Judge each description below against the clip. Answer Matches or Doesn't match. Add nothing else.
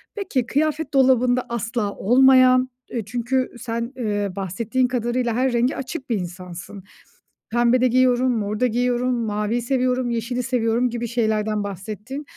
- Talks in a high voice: Matches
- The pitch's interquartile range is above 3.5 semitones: Doesn't match